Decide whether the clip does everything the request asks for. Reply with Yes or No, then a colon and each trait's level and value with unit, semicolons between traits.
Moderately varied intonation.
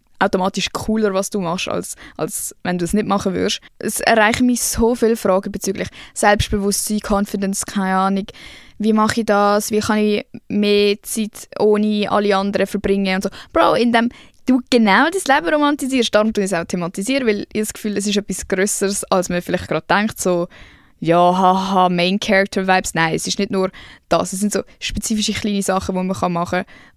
No: narrow, 2.1 semitones